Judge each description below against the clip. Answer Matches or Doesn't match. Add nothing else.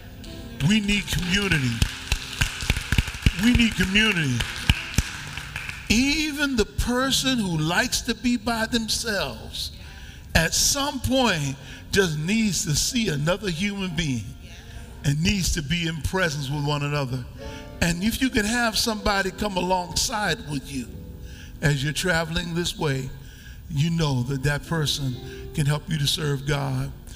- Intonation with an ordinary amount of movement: Doesn't match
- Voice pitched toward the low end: Doesn't match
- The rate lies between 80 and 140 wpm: Matches